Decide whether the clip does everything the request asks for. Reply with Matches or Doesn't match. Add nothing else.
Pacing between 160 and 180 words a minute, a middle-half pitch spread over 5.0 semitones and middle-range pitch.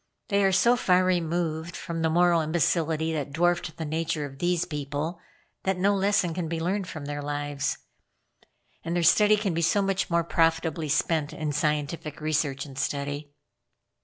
Doesn't match